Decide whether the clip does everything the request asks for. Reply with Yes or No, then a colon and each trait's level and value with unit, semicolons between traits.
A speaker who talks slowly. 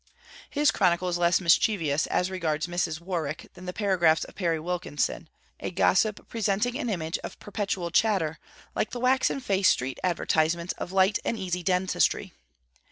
No: average, 160 wpm